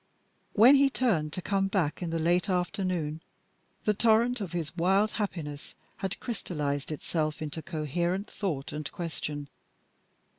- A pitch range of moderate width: Yes, average, 4.5 semitones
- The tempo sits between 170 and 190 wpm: No, average, 140 wpm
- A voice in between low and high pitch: Yes, medium, 175 Hz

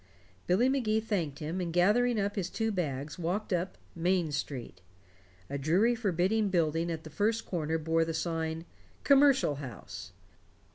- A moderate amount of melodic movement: Yes, average, 5.0 semitones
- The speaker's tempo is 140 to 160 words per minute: Yes, average, 150 wpm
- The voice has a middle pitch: Yes, medium, 175 Hz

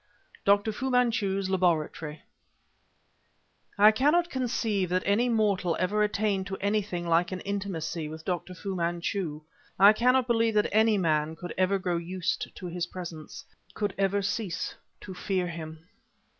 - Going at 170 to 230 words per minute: No, average, 150 wpm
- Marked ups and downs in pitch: No, average, 3.4 semitones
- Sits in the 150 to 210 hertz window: Yes, high, 190 Hz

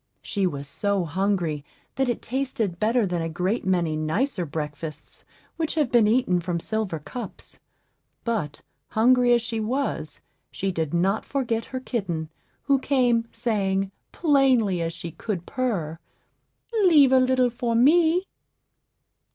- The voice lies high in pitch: Yes, high, 220 Hz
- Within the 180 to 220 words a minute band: No, average, 140 wpm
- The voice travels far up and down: Yes, wide, 6.6 semitones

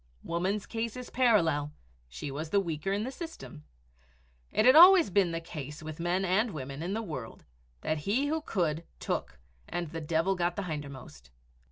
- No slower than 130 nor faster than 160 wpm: No, average, 180 wpm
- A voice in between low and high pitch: Yes, medium, 175 Hz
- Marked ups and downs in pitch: Yes, wide, 5.8 semitones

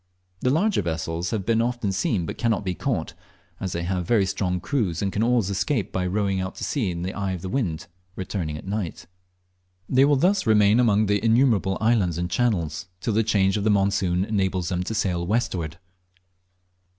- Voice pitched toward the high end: No, low, 100 Hz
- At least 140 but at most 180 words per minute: No, average, 200 wpm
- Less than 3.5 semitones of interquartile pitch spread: No, average, 3.8 semitones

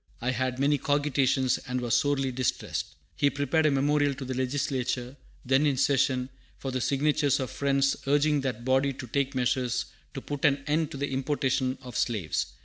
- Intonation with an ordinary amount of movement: No, narrow, 1.8 semitones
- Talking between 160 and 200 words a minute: Yes, average, 180 wpm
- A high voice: No, low, 135 Hz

